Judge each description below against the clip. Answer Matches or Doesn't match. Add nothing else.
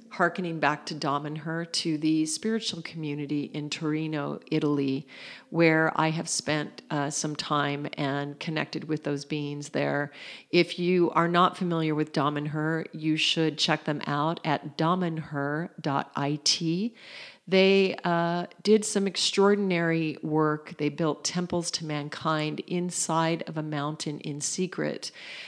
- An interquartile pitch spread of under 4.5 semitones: Matches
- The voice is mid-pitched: Matches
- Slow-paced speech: Matches